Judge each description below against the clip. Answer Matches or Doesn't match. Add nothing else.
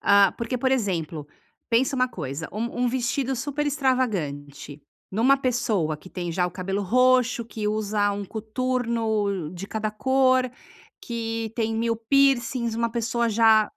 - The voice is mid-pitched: Doesn't match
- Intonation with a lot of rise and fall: Doesn't match